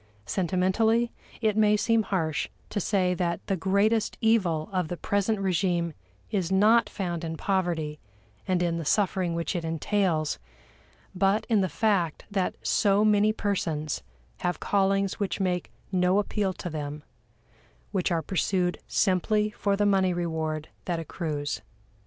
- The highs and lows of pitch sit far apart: No, average, 3.3 semitones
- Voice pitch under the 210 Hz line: Yes, medium, 185 Hz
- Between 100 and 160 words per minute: Yes, average, 145 wpm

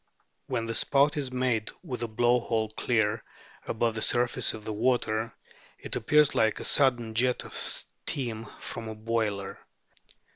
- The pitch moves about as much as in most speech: No, narrow, 2.2 semitones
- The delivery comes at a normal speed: Yes, average, 155 wpm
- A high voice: No, low, 115 Hz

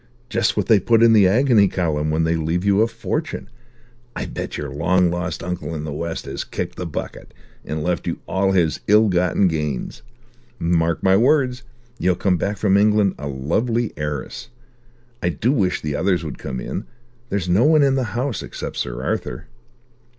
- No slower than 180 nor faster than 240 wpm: Yes, average, 185 wpm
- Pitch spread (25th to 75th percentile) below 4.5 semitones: No, average, 5.0 semitones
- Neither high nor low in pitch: No, very low, 90 Hz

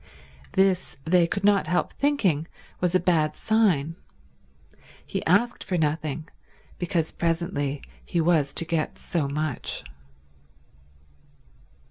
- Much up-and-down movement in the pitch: No, average, 3.1 semitones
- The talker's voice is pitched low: No, medium, 170 Hz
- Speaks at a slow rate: Yes, slow, 110 wpm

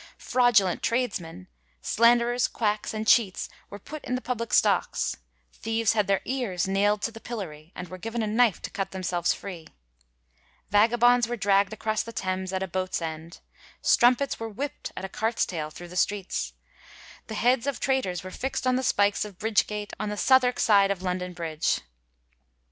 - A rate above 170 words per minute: Yes, average, 180 wpm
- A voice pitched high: Yes, high, 210 Hz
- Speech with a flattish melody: No, average, 4.2 semitones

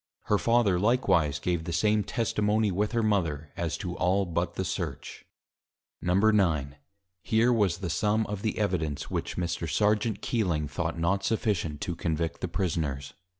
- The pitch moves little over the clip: No, average, 4.3 semitones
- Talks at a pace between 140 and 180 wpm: Yes, average, 155 wpm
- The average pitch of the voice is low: Yes, very low, 95 Hz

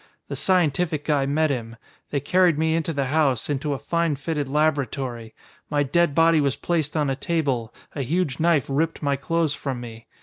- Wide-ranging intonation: No, average, 3.2 semitones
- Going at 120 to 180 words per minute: No, average, 190 wpm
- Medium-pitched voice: Yes, medium, 145 Hz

